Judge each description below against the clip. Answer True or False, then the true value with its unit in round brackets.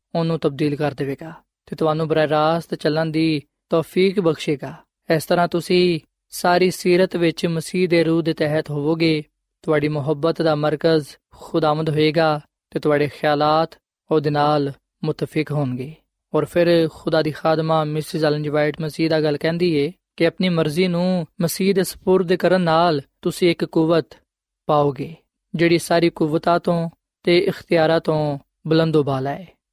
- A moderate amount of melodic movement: False (2.1 semitones)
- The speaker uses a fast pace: False (150 wpm)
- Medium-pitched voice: True (160 Hz)